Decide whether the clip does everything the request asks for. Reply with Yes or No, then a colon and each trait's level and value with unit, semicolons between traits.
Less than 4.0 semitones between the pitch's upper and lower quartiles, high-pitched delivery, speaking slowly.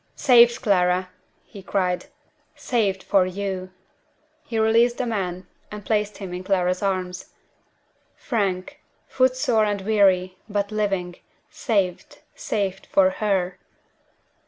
Yes: average, 2.9 semitones; high, 195 Hz; slow, 115 wpm